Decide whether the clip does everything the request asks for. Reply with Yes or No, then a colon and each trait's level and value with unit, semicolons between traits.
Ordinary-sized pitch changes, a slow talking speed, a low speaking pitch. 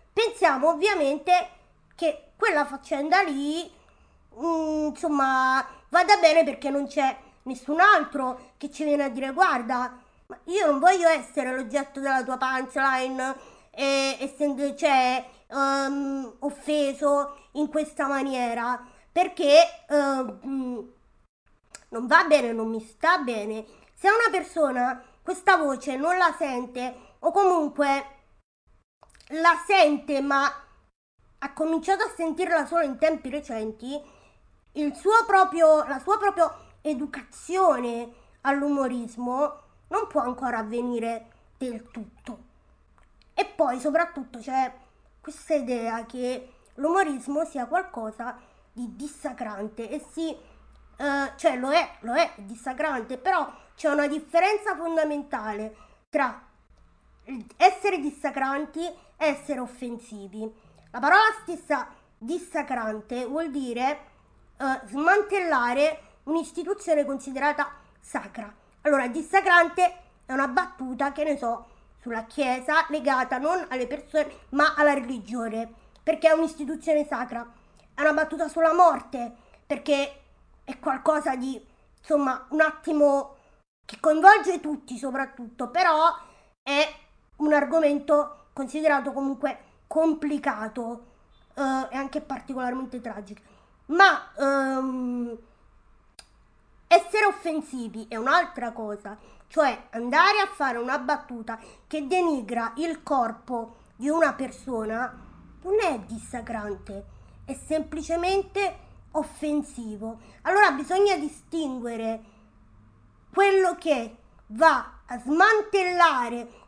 No: average, 4.3 semitones; slow, 105 wpm; very high, 285 Hz